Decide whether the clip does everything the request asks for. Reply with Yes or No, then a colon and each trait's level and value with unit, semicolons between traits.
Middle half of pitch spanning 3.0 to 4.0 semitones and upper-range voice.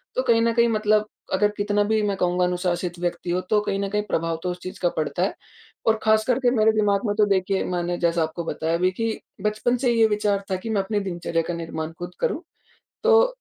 Yes: average, 3.6 semitones; high, 200 Hz